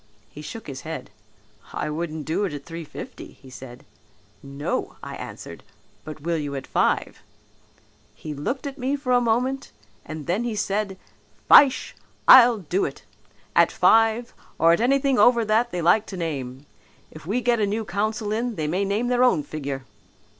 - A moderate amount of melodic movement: No, wide, 7.4 semitones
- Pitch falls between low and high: No, high, 200 Hz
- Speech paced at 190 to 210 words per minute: No, average, 175 wpm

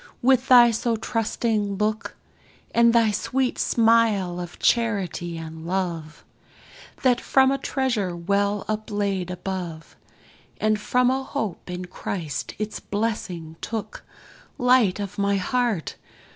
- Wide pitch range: No, average, 4.5 semitones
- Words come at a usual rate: No, slow, 120 wpm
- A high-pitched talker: Yes, high, 210 Hz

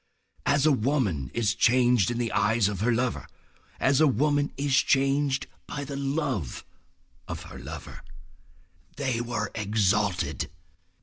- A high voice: No, low, 125 Hz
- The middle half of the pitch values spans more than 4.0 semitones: Yes, average, 4.8 semitones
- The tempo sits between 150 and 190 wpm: No, slow, 135 wpm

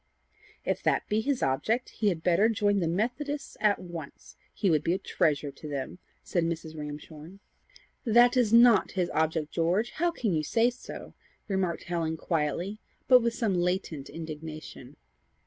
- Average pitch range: No, wide, 5.8 semitones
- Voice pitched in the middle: Yes, medium, 180 Hz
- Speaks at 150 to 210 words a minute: Yes, average, 165 wpm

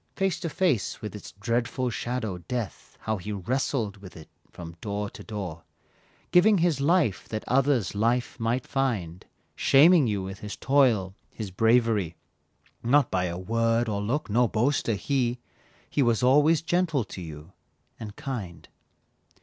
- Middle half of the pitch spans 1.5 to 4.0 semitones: No, average, 5.1 semitones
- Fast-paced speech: No, average, 150 wpm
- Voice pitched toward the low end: Yes, low, 115 Hz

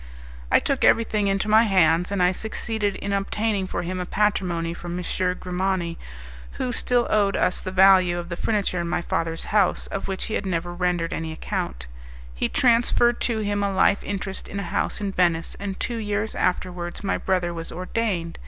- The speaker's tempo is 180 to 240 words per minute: Yes, average, 190 wpm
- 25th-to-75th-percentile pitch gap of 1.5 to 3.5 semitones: Yes, average, 2.8 semitones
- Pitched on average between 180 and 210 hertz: Yes, high, 190 Hz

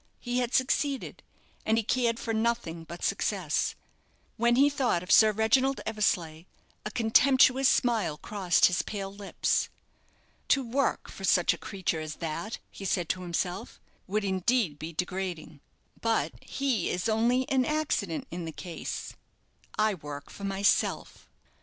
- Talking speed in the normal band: Yes, average, 145 wpm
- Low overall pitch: No, high, 210 Hz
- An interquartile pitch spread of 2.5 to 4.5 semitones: No, wide, 5.5 semitones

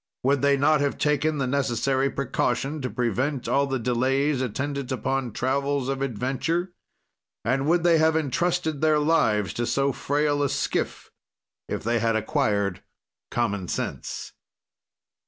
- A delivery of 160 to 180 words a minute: No, average, 140 wpm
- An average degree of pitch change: Yes, average, 3.0 semitones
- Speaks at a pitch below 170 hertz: Yes, low, 135 Hz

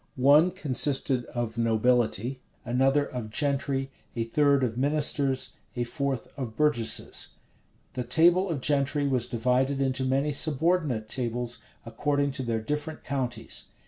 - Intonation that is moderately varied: Yes, average, 3.0 semitones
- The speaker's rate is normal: No, slow, 130 wpm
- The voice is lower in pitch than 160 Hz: Yes, low, 135 Hz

